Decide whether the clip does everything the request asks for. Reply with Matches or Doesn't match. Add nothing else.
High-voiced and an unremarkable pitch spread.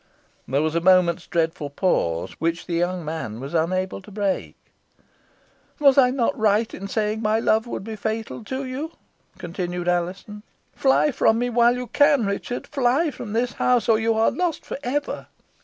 Doesn't match